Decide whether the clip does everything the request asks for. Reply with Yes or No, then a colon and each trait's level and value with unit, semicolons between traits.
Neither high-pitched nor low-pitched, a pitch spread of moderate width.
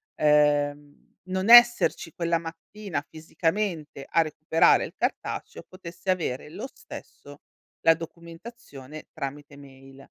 Yes: medium, 165 Hz; average, 4.1 semitones